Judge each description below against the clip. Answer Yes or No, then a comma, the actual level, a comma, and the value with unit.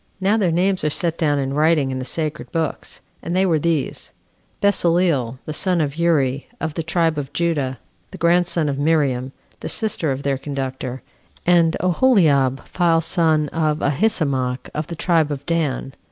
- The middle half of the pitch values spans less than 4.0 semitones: Yes, average, 3.5 semitones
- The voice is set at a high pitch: No, medium, 155 Hz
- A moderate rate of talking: Yes, average, 170 wpm